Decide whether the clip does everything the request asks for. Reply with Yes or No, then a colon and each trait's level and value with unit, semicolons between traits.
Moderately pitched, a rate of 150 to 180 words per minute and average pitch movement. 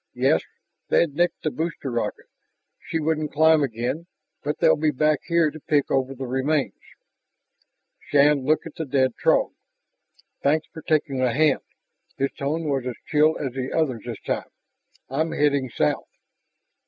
Yes: medium, 145 Hz; average, 155 wpm; average, 3.0 semitones